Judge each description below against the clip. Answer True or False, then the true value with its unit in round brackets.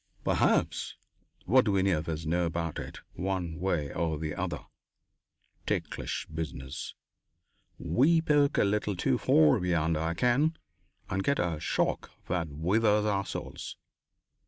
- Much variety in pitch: False (4.6 semitones)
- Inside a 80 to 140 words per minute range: True (135 wpm)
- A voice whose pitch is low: True (90 Hz)